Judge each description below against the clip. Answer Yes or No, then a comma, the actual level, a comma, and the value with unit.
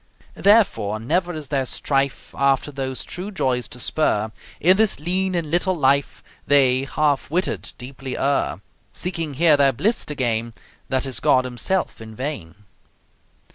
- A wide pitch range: No, average, 5.0 semitones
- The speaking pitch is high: No, medium, 140 Hz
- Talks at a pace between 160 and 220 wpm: No, average, 150 wpm